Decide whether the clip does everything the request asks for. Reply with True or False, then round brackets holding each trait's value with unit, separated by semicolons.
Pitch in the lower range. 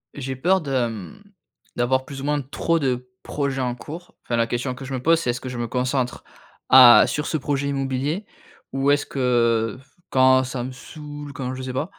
True (130 Hz)